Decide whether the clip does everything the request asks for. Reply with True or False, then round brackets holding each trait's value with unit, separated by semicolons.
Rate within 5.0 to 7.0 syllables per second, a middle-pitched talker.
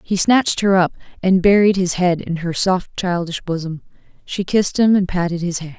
True (5.3 syllables/s; 180 Hz)